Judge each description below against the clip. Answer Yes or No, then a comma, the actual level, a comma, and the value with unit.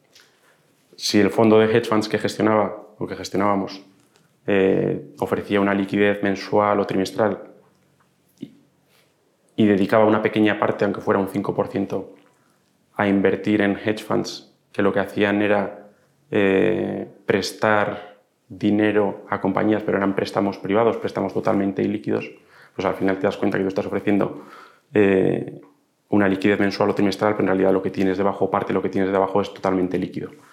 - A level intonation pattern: Yes, narrow, 1.4 semitones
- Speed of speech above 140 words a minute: Yes, average, 155 wpm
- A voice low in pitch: Yes, low, 100 Hz